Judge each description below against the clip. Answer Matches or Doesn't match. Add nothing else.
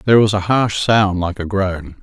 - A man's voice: Matches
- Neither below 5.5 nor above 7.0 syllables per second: Doesn't match